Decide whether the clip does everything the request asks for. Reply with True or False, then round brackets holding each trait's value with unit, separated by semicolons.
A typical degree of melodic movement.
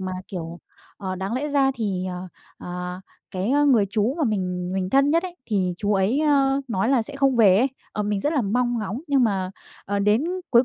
False (6.2 semitones)